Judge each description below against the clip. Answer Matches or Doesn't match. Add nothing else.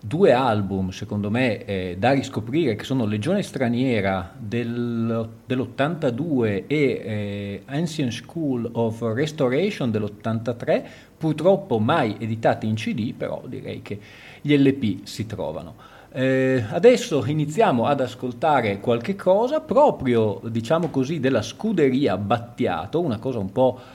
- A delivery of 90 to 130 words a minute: Matches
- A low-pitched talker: Matches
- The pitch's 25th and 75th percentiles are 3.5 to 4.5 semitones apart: Matches